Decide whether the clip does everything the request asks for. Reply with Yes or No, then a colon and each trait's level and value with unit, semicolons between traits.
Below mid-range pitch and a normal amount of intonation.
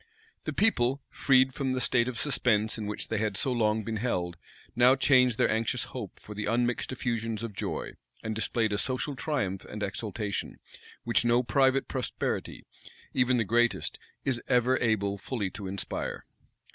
Yes: low, 115 Hz; average, 3.1 semitones